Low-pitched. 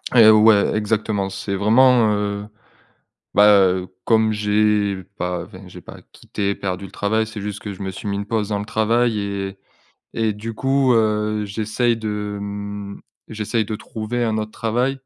Yes: low, 105 Hz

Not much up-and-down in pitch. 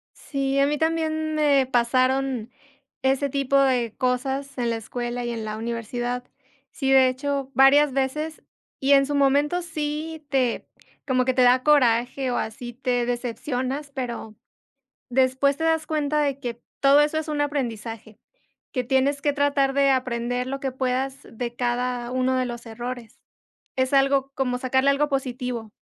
Yes: narrow, 2.3 semitones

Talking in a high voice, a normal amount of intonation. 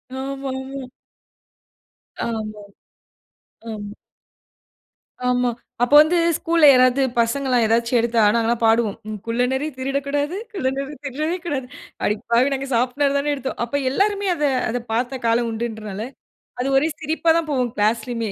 Yes: very high, 255 Hz; average, 3.3 semitones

